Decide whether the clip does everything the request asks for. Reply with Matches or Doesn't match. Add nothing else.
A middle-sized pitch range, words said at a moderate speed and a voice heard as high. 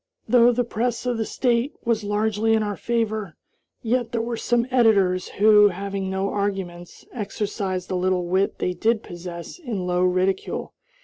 Matches